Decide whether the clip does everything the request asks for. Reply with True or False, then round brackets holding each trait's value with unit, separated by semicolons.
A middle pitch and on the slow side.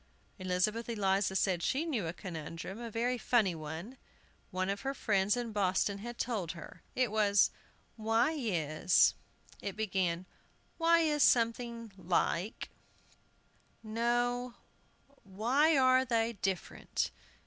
False (215 Hz; 125 wpm)